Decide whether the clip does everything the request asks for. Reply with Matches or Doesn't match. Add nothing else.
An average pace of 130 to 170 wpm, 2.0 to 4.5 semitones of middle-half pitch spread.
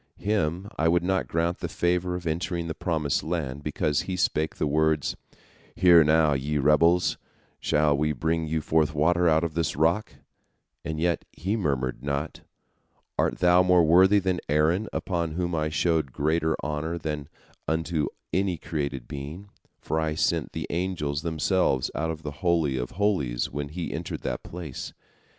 Matches